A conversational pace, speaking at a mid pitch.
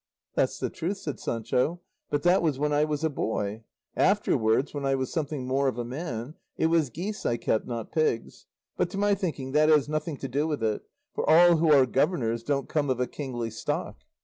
No: fast, 215 wpm; medium, 145 Hz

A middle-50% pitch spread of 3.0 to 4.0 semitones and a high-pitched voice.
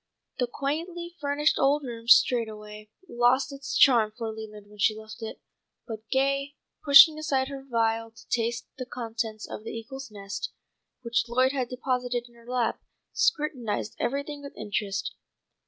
Yes: average, 3.7 semitones; high, 240 Hz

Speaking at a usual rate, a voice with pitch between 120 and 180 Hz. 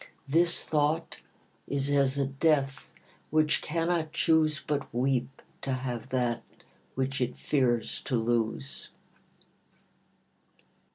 No: slow, 105 wpm; medium, 140 Hz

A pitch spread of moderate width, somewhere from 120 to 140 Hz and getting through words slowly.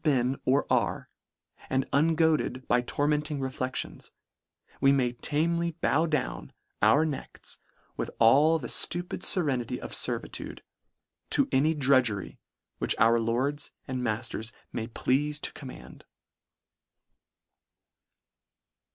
Yes: average, 3.5 semitones; low, 135 Hz; slow, 115 wpm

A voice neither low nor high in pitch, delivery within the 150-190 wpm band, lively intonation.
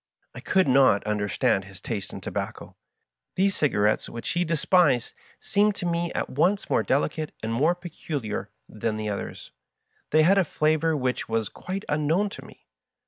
Yes: medium, 150 Hz; average, 165 wpm; wide, 7.5 semitones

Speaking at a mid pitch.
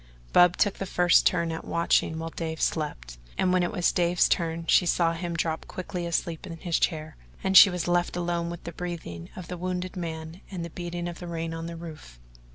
Yes: medium, 170 Hz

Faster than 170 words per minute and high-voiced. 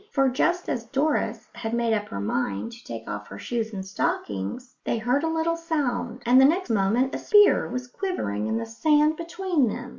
Yes: fast, 205 wpm; high, 245 Hz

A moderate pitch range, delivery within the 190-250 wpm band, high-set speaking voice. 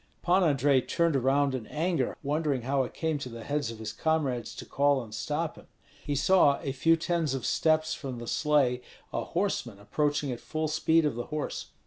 No: average, 3.8 semitones; average, 200 wpm; medium, 145 Hz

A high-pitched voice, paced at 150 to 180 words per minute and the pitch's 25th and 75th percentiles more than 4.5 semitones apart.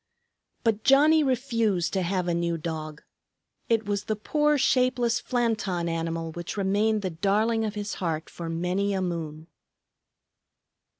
No: high, 200 Hz; average, 140 wpm; average, 5.0 semitones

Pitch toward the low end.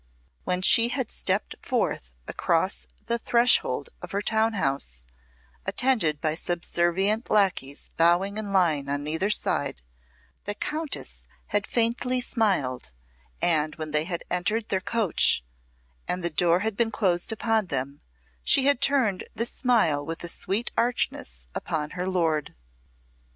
No: medium, 185 Hz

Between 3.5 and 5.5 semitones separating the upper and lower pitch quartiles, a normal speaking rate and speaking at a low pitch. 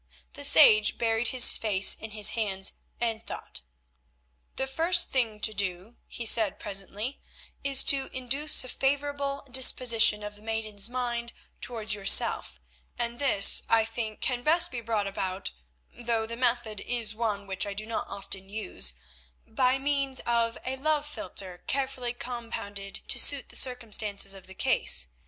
No: average, 3.9 semitones; average, 150 wpm; high, 225 Hz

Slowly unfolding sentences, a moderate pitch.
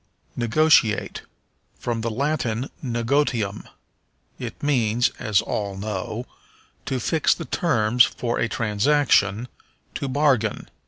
No: slow, 105 wpm; low, 120 Hz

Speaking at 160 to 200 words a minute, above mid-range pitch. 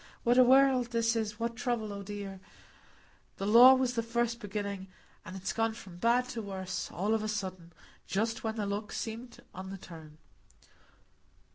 Yes: average, 170 wpm; high, 220 Hz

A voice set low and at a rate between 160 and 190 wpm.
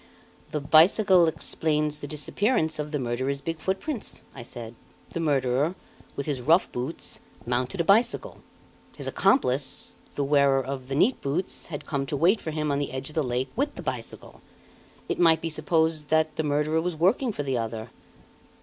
No: medium, 150 Hz; average, 185 wpm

